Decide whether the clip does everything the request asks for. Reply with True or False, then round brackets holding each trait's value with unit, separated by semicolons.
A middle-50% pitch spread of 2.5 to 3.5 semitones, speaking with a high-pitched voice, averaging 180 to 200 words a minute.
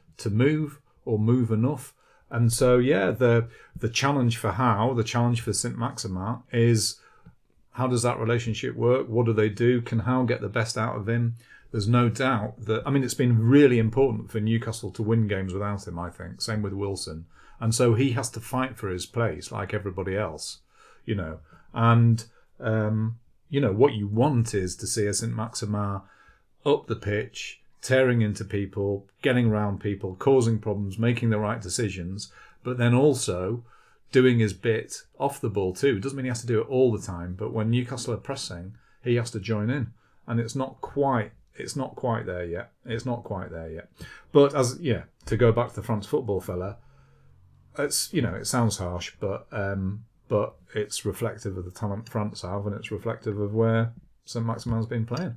False (2.9 semitones; 115 Hz; 195 wpm)